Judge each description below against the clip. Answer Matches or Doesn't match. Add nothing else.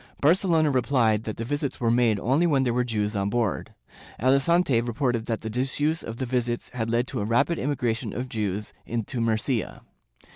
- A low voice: Matches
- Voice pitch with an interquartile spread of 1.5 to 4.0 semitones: Matches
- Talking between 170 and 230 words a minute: Matches